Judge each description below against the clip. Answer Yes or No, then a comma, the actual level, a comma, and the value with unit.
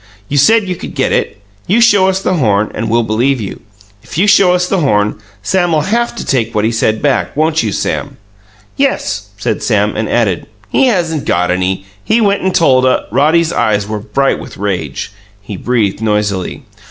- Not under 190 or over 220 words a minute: Yes, average, 200 wpm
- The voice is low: Yes, low, 130 Hz